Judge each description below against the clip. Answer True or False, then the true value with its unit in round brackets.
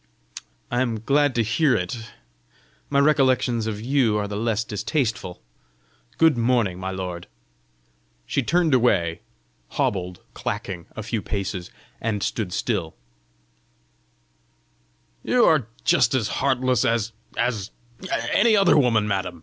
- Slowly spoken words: True (125 wpm)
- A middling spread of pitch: True (4.6 semitones)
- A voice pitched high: False (115 Hz)